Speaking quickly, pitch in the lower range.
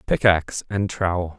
No: slow, 130 wpm; very low, 90 Hz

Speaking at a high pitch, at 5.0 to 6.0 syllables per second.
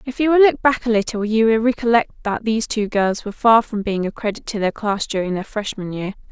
Yes: high, 220 Hz; 5.9 syllables/s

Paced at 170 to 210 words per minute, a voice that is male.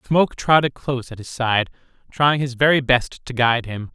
Yes: average, 200 wpm; male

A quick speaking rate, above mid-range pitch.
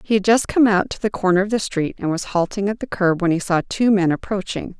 Yes: fast, 290 wpm; high, 195 Hz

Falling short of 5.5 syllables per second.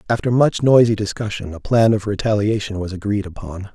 No: 5.6 syllables/s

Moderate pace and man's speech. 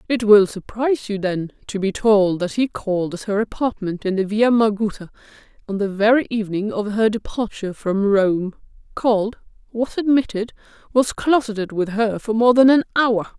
No: average, 175 wpm; female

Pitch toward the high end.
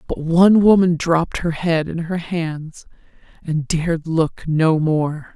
No: medium, 165 Hz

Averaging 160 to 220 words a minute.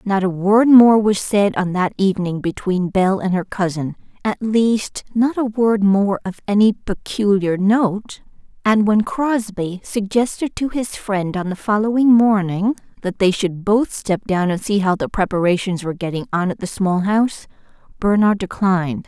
Yes: average, 175 wpm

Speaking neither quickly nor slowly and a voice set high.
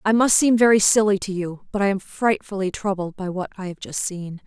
No: fast, 240 wpm; high, 195 Hz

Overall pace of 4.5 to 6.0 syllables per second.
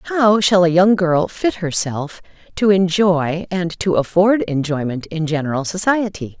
No: 4.2 syllables/s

